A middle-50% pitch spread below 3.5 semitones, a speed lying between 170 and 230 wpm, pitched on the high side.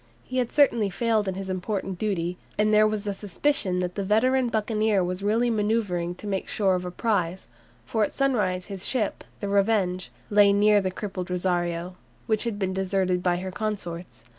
Yes: average, 2.9 semitones; average, 190 wpm; high, 200 Hz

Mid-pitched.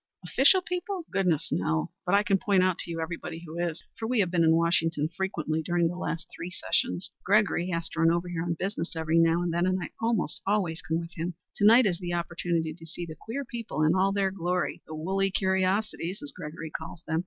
Yes: medium, 175 Hz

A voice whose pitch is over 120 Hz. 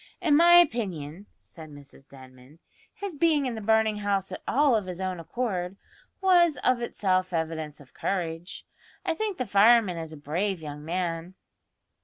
Yes: high, 190 Hz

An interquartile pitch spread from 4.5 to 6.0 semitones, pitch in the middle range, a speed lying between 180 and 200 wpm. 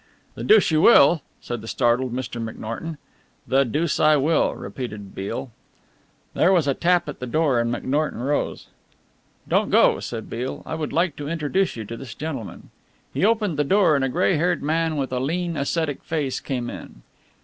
Yes: average, 4.8 semitones; medium, 145 Hz; average, 185 wpm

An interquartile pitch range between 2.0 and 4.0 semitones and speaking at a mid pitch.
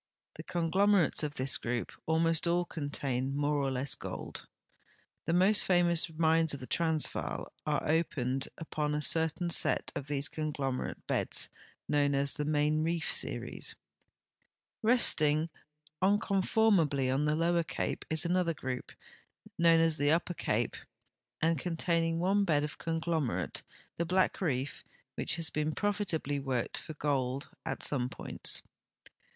Yes: average, 3.0 semitones; medium, 155 Hz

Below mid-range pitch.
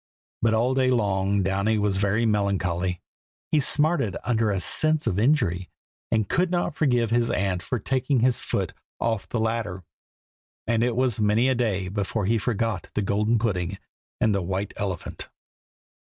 Yes: low, 110 Hz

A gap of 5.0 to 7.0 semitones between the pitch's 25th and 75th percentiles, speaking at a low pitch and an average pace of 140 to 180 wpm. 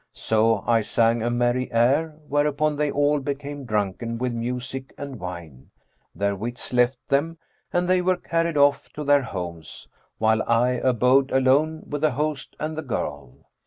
No: average, 4.2 semitones; low, 130 Hz; average, 160 wpm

